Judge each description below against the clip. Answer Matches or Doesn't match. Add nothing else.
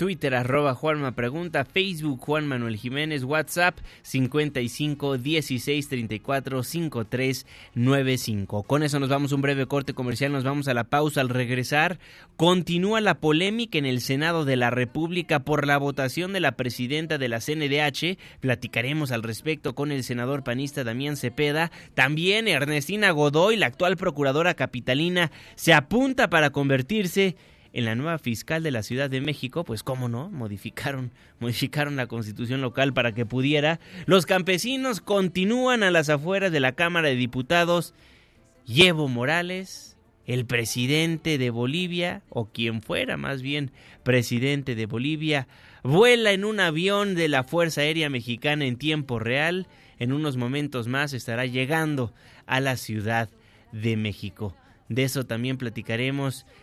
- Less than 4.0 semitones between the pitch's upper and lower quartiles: Doesn't match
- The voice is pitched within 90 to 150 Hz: Matches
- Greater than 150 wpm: Doesn't match